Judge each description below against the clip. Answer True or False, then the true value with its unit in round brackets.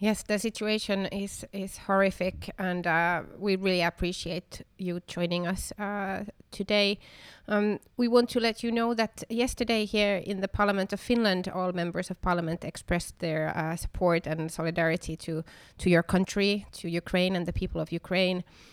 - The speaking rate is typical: False (165 wpm)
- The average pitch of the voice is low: False (185 Hz)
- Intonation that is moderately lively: True (3.0 semitones)